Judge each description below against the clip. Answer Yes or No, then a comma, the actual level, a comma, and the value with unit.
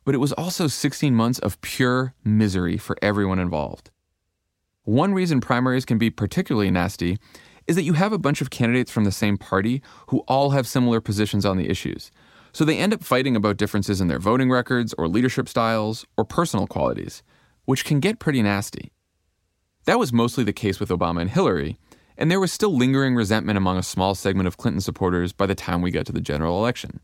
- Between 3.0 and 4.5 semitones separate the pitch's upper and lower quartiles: No, wide, 5.4 semitones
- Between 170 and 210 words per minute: Yes, fast, 205 wpm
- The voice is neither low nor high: No, low, 110 Hz